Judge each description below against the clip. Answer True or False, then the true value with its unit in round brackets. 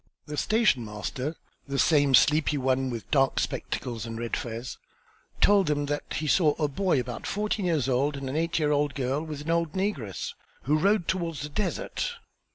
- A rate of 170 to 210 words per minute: True (185 wpm)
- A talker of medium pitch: True (145 Hz)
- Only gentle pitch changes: False (4.1 semitones)